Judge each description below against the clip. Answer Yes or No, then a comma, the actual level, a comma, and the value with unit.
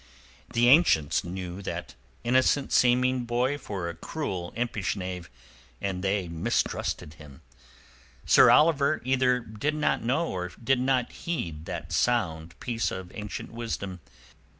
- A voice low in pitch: Yes, low, 110 Hz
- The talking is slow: Yes, slow, 130 wpm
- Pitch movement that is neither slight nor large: No, wide, 6.0 semitones